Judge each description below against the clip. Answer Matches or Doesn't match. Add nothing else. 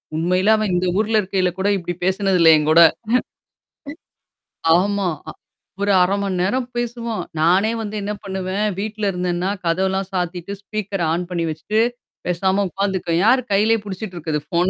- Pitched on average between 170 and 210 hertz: Matches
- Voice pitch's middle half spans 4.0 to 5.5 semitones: Doesn't match